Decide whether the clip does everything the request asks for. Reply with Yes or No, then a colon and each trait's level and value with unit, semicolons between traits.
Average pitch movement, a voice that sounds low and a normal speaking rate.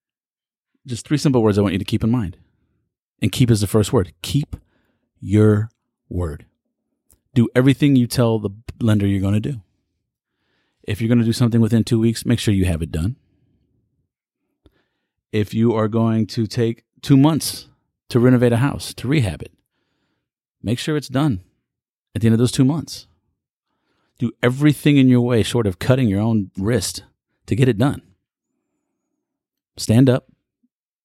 Yes: average, 3.9 semitones; low, 115 Hz; average, 170 wpm